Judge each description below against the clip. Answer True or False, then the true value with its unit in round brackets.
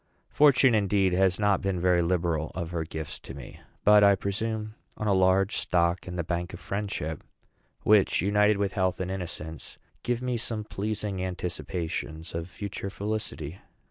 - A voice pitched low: True (95 Hz)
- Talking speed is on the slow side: False (165 wpm)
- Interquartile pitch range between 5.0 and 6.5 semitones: False (3.2 semitones)